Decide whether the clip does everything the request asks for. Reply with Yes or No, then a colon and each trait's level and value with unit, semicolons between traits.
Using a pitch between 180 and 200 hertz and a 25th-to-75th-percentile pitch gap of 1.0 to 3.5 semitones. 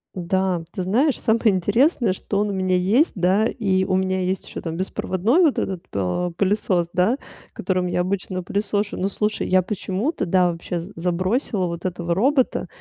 Yes: high, 190 Hz; average, 2.7 semitones